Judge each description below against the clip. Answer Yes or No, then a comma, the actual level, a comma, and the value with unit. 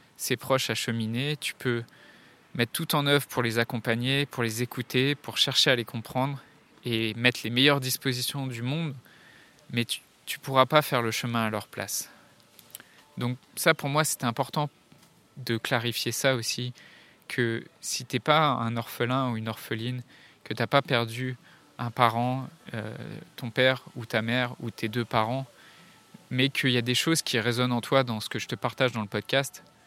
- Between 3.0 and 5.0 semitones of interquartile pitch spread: No, narrow, 2.5 semitones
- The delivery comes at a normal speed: Yes, average, 190 wpm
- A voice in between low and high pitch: No, low, 125 Hz